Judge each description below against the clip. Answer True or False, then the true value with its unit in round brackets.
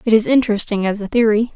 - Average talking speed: False (230 wpm)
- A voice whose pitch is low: False (220 Hz)